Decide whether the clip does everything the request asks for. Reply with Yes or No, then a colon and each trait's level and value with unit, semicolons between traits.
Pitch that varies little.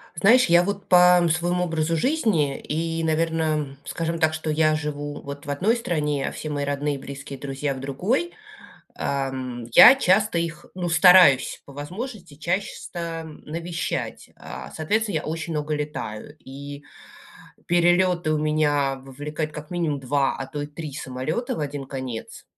No: average, 3.4 semitones